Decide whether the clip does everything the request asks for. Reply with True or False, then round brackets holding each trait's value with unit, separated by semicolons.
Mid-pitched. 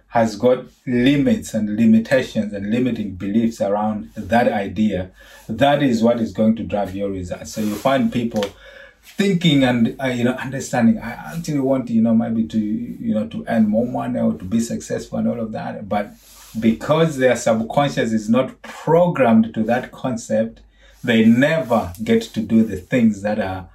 False (120 Hz)